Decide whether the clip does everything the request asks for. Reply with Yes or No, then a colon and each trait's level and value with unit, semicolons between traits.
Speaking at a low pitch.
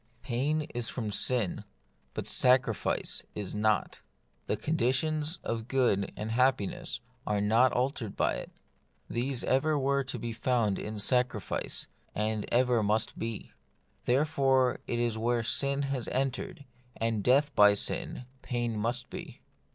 Yes: low, 120 Hz